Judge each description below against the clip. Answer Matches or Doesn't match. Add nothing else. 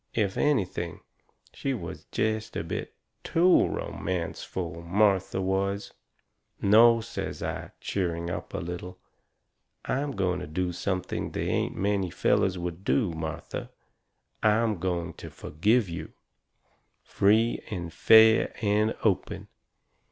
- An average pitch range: Matches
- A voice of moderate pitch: Doesn't match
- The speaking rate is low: Matches